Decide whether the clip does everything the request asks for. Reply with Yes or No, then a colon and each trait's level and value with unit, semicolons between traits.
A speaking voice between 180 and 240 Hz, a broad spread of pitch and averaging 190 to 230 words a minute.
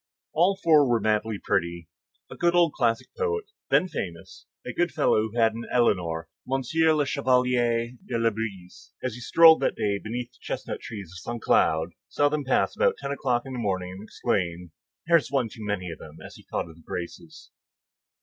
No: low, 115 Hz; wide, 6.5 semitones; average, 200 wpm